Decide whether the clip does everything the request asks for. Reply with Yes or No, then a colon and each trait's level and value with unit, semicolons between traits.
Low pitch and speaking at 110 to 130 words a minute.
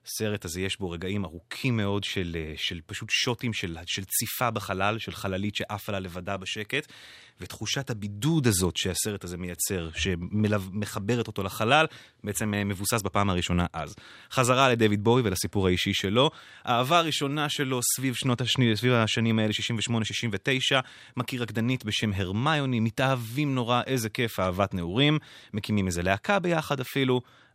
No: low, 110 Hz; average, 145 wpm